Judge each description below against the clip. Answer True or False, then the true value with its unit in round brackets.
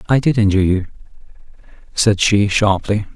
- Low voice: True (105 Hz)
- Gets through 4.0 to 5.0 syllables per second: False (5.4 syllables/s)